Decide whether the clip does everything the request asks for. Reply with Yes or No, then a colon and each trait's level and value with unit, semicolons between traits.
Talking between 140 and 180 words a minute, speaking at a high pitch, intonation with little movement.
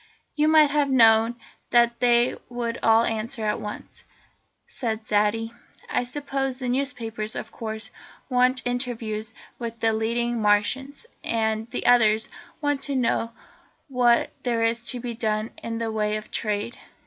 Yes: average, 150 wpm; high, 230 Hz; narrow, 2.1 semitones